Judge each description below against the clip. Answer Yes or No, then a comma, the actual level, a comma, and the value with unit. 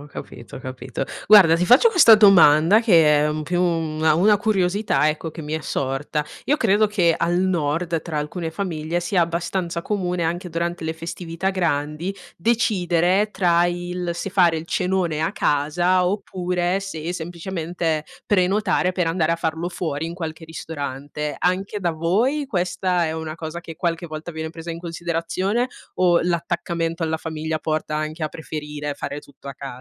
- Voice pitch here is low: No, medium, 170 Hz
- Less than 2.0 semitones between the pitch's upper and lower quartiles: No, narrow, 2.4 semitones